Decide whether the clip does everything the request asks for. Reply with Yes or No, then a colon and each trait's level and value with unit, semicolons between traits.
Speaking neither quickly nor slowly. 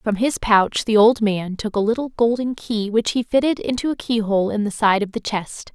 No: fast, 250 wpm